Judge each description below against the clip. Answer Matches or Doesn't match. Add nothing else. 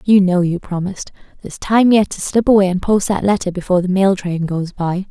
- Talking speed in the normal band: Doesn't match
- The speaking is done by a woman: Matches